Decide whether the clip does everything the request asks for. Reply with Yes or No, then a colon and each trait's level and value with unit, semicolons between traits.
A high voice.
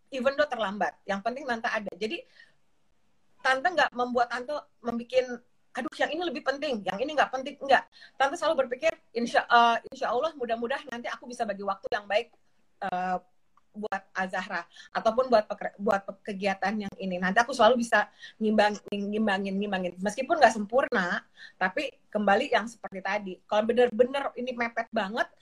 Yes: high, 235 Hz